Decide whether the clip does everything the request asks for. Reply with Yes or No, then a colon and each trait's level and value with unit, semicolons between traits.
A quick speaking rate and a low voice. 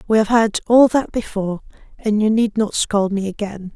No: fast, 210 wpm; high, 210 Hz